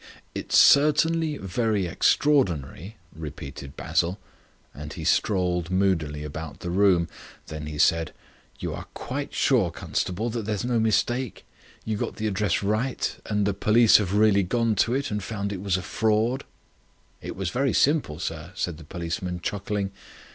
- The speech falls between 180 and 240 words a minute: No, average, 155 wpm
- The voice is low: Yes, low, 100 Hz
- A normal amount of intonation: Yes, average, 4.6 semitones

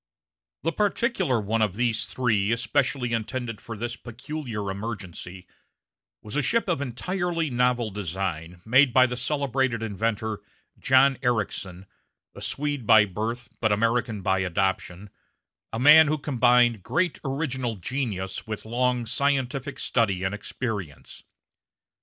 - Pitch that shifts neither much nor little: Yes, average, 4.2 semitones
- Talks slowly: Yes, slow, 130 wpm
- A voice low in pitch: Yes, low, 120 Hz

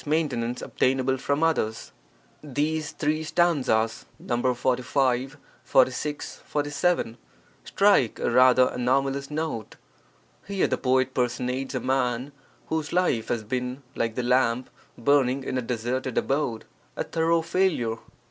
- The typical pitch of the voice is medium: No, low, 130 Hz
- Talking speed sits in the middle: No, slow, 120 wpm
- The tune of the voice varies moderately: Yes, average, 3.2 semitones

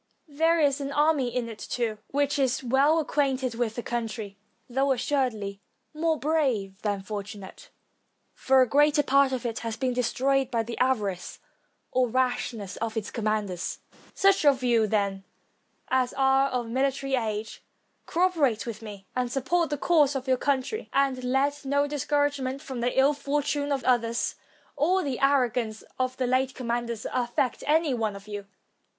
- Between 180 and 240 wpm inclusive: No, average, 165 wpm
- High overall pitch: Yes, very high, 255 Hz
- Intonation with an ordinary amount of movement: Yes, average, 3.6 semitones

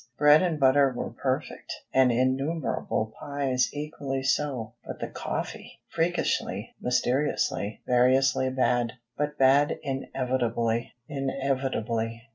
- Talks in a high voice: No, low, 130 Hz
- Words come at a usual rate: No, slow, 95 wpm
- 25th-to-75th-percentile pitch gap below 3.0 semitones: Yes, narrow, 2.6 semitones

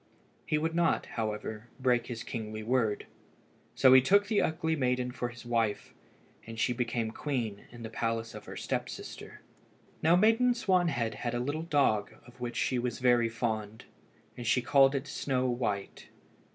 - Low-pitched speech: Yes, low, 125 Hz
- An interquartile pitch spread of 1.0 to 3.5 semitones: No, average, 4.0 semitones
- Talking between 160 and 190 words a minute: Yes, average, 170 wpm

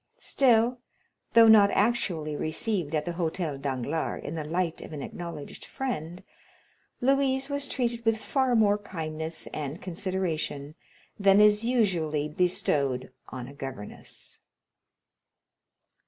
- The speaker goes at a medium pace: No, slow, 120 wpm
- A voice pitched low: No, medium, 175 Hz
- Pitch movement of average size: No, wide, 6.6 semitones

